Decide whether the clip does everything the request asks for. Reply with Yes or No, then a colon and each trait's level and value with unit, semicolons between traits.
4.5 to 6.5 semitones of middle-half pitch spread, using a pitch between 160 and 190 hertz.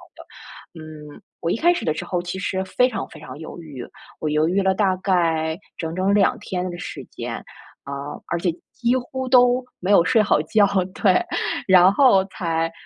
No: average, 4.1 semitones; medium, 185 Hz